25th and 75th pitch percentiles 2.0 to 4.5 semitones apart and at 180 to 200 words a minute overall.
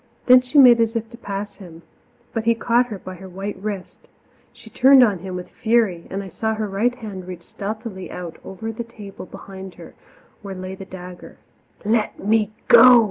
Yes: average, 3.4 semitones; average, 195 wpm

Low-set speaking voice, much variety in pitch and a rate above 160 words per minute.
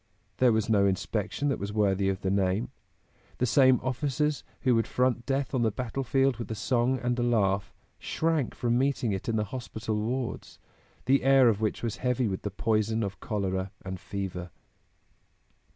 No: low, 115 Hz; average, 4.3 semitones; average, 180 wpm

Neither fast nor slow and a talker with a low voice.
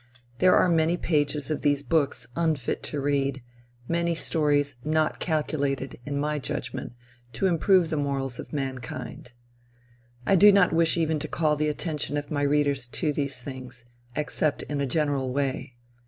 No: average, 160 wpm; medium, 145 Hz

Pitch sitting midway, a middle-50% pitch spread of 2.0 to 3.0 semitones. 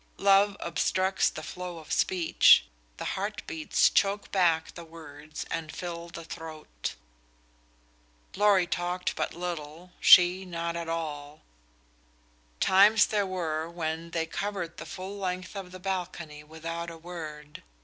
Yes: medium, 170 Hz; narrow, 2.6 semitones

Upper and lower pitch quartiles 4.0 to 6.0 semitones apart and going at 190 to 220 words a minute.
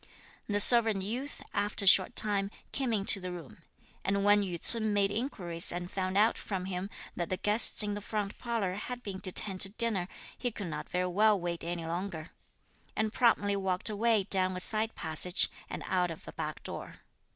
No: average, 2.9 semitones; average, 195 wpm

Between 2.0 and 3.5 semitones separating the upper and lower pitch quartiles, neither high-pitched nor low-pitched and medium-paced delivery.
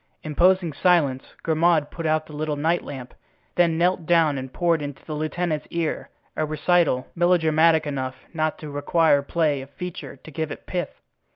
Yes: average, 2.7 semitones; medium, 155 Hz; average, 170 wpm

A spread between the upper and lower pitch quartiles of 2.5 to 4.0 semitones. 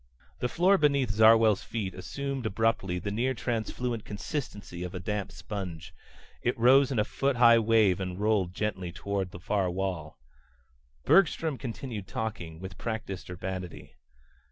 No: average, 4.5 semitones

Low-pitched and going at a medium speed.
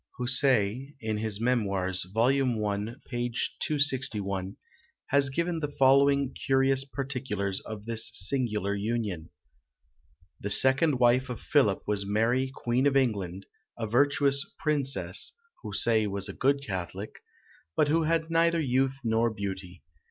No: low, 120 Hz; slow, 130 wpm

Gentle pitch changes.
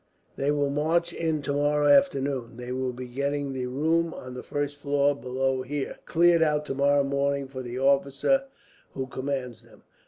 Yes: narrow, 2.0 semitones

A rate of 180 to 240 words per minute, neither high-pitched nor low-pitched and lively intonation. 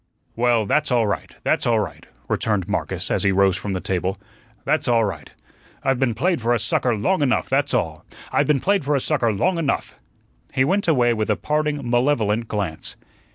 No: average, 200 wpm; low, 120 Hz; wide, 5.8 semitones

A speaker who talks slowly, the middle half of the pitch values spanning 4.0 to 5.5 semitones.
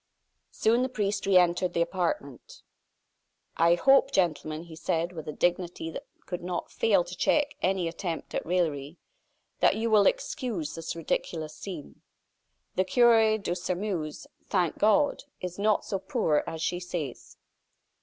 No: average, 150 wpm; average, 4.3 semitones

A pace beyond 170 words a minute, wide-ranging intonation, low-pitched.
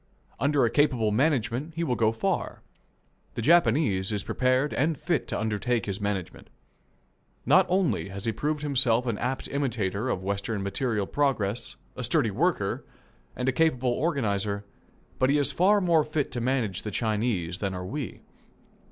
No: average, 160 wpm; wide, 5.8 semitones; low, 120 Hz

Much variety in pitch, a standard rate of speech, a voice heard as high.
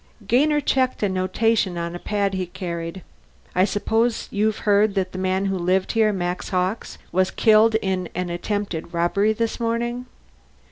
No: average, 3.2 semitones; average, 160 wpm; high, 195 Hz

